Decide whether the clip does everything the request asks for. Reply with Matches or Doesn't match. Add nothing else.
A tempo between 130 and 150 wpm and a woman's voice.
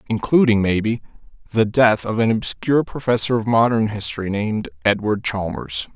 Doesn't match